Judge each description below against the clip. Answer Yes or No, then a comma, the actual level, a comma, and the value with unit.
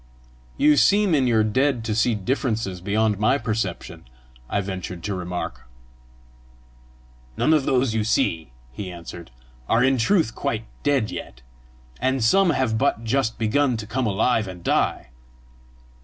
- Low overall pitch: Yes, low, 110 Hz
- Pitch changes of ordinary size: Yes, average, 4.8 semitones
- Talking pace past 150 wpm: No, average, 145 wpm